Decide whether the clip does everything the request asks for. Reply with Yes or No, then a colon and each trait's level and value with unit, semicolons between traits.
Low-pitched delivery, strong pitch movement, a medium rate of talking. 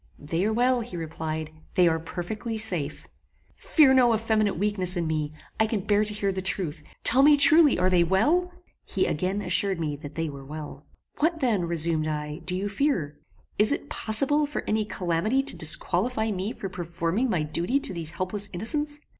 No: high, 190 Hz; wide, 5.8 semitones; average, 190 wpm